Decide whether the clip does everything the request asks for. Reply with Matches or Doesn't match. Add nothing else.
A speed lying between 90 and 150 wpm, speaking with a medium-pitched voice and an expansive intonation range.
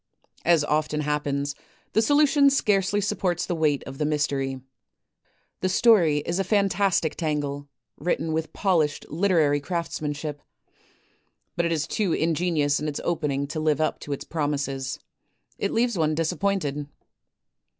Doesn't match